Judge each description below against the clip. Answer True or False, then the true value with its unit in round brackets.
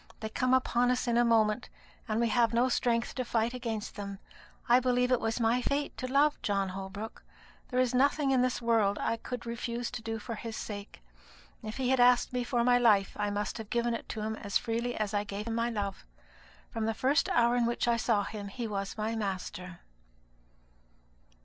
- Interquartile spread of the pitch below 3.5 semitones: True (2.6 semitones)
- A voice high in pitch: True (230 Hz)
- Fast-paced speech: True (215 wpm)